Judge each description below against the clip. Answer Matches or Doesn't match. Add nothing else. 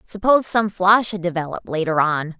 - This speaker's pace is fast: Doesn't match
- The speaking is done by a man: Doesn't match